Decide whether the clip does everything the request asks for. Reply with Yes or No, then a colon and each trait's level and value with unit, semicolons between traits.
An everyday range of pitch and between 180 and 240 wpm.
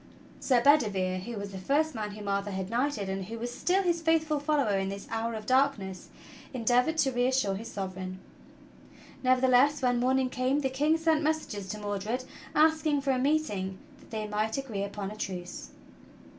No: wide, 5.9 semitones; average, 185 wpm